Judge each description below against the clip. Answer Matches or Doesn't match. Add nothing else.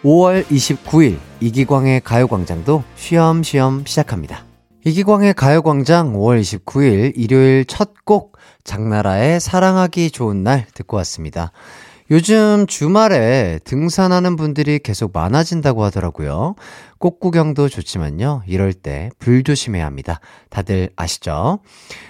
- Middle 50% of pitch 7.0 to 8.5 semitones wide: Matches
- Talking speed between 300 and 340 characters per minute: Doesn't match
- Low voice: Matches